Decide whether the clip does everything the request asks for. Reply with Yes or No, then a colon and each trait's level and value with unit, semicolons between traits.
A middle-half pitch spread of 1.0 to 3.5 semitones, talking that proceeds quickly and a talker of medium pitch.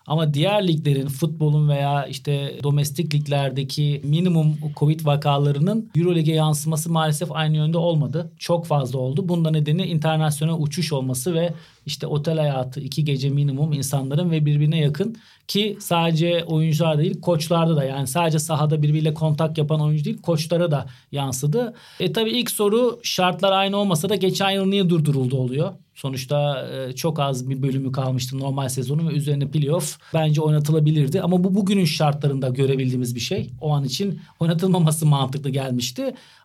Yes: average, 3.1 semitones; fast, 150 wpm; medium, 155 Hz